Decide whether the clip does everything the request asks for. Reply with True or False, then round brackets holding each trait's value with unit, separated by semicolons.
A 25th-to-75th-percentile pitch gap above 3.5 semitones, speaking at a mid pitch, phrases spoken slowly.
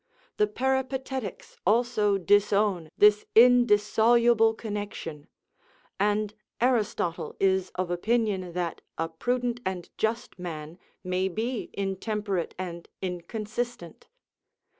False (4.3 semitones; 210 Hz; 95 wpm)